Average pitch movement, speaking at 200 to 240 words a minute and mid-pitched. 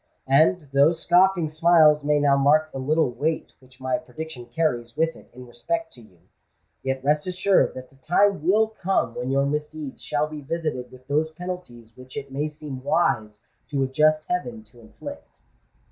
No: average, 3.8 semitones; average, 180 wpm; medium, 150 Hz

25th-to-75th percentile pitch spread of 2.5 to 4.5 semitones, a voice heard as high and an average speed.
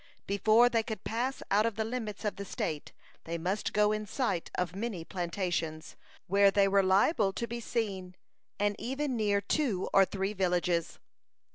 Yes: average, 3.2 semitones; high, 200 Hz; average, 170 wpm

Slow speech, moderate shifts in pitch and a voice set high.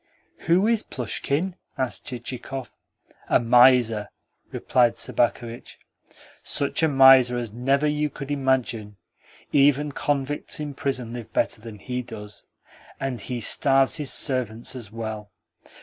No: slow, 125 wpm; average, 3.0 semitones; low, 130 Hz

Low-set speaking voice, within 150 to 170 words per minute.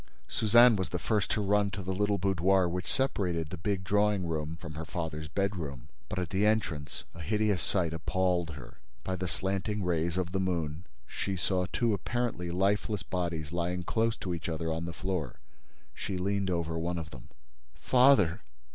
No: very low, 90 Hz; average, 180 wpm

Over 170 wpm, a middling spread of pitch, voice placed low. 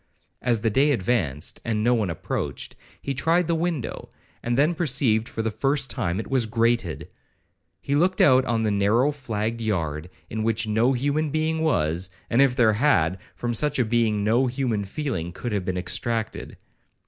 Yes: average, 180 wpm; average, 4.5 semitones; low, 115 Hz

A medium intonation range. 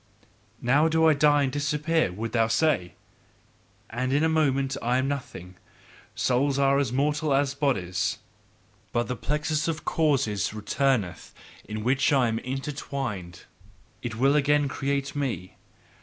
Yes: average, 4.1 semitones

